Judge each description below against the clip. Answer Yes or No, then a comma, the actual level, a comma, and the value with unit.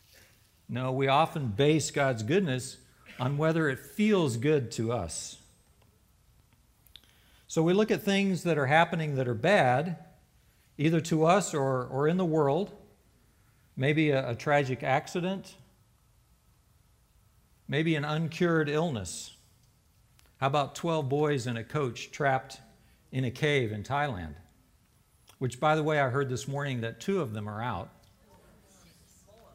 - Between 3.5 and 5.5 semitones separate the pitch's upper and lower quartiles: Yes, average, 4.2 semitones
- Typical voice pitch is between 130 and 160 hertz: Yes, medium, 140 Hz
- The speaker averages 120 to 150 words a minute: Yes, average, 140 wpm